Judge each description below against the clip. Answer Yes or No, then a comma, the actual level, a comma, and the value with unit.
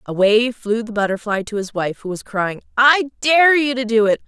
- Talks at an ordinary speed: No, fast, 225 wpm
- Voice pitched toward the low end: No, high, 230 Hz